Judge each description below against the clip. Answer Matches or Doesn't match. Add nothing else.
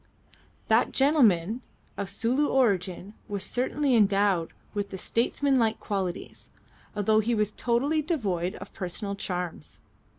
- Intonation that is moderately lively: Matches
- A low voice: Doesn't match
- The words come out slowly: Matches